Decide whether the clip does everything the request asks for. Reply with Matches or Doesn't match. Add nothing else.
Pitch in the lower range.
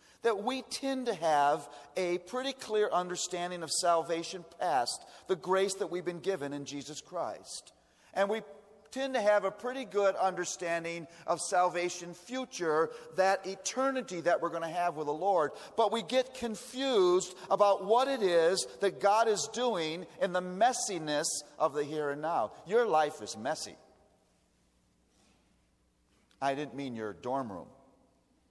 Doesn't match